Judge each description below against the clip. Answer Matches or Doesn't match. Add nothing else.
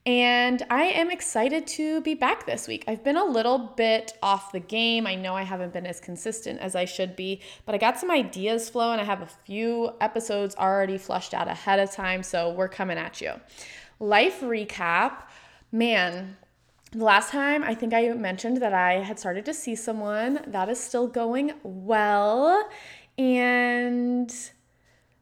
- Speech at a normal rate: Matches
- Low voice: Doesn't match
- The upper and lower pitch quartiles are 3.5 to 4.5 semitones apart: Matches